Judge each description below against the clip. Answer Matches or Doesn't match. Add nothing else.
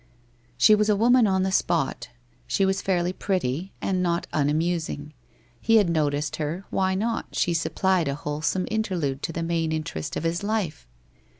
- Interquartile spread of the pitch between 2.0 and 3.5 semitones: Doesn't match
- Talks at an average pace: Matches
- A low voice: Doesn't match